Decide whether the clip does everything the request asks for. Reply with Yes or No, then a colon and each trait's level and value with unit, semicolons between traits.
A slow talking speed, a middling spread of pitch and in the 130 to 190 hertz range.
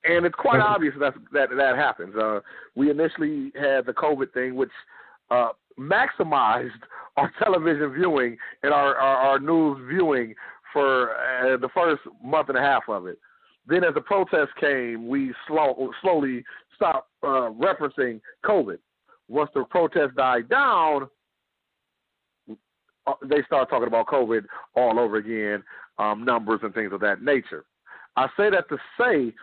No: average, 150 wpm; average, 4.1 semitones; low, 135 Hz